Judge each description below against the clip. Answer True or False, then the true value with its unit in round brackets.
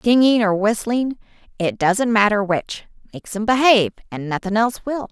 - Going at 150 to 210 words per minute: False (140 wpm)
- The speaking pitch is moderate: False (215 Hz)